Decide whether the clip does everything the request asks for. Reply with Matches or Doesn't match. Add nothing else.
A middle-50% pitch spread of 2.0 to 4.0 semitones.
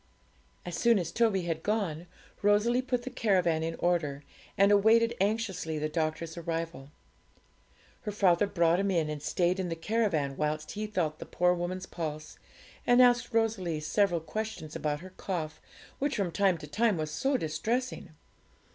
Doesn't match